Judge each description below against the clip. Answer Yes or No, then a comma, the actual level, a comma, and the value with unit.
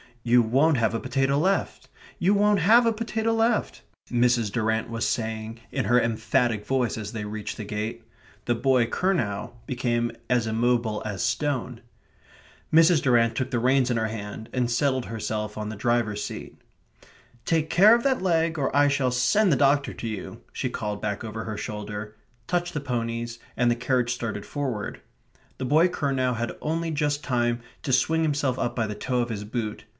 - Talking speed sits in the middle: Yes, average, 185 wpm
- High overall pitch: No, low, 120 Hz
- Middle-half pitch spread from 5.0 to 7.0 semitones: No, average, 4.5 semitones